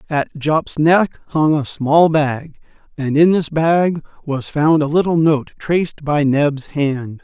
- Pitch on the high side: No, medium, 150 Hz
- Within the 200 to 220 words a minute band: No, average, 165 wpm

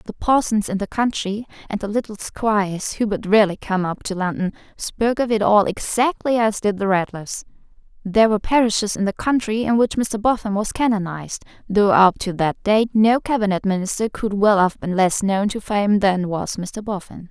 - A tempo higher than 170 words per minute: Yes, average, 200 wpm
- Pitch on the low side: No, high, 205 Hz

